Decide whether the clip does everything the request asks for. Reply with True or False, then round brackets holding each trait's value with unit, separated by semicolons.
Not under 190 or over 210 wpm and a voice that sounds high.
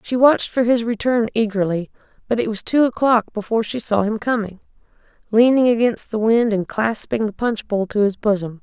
True (195 wpm; 220 Hz)